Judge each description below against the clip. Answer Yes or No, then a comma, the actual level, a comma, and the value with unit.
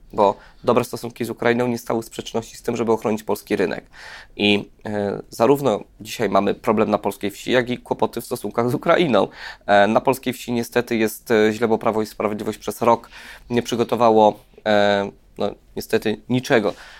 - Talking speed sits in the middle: No, fast, 175 wpm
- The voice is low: Yes, low, 115 Hz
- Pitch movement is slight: Yes, narrow, 2.1 semitones